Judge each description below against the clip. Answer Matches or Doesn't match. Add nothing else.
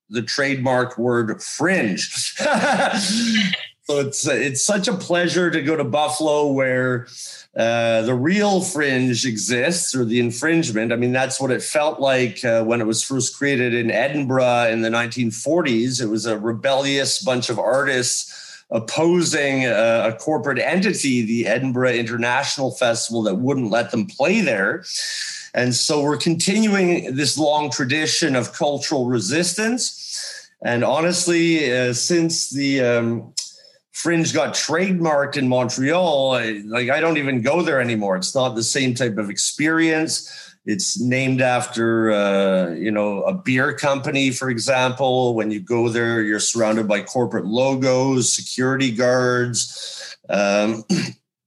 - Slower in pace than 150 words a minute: Matches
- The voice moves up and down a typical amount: Matches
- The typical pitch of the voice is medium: Doesn't match